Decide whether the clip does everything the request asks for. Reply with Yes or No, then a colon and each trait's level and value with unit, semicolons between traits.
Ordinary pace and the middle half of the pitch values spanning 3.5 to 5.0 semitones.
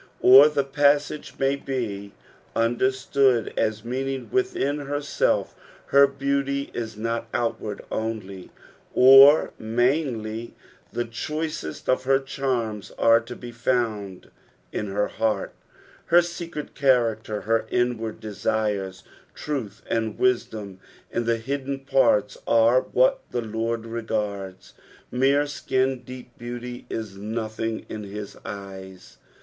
No: slow, 120 wpm; average, 3.8 semitones